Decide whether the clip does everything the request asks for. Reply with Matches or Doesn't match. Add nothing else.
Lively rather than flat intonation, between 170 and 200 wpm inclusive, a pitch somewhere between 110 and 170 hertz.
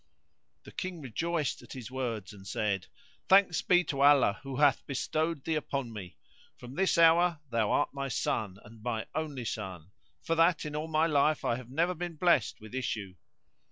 Matches